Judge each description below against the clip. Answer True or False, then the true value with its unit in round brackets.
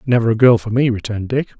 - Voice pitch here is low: True (115 Hz)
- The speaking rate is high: True (265 wpm)